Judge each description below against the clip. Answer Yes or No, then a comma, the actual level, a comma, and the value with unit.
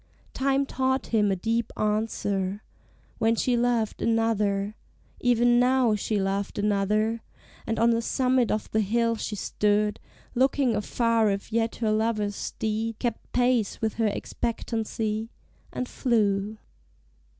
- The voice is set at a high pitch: Yes, high, 225 Hz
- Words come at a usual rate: No, slow, 130 wpm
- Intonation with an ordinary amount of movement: No, narrow, 2.1 semitones